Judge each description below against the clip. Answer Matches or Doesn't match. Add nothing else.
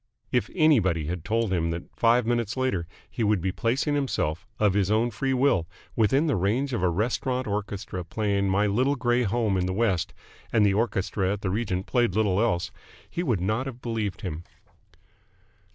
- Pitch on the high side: Doesn't match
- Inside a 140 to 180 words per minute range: Doesn't match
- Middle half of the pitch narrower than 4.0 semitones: Doesn't match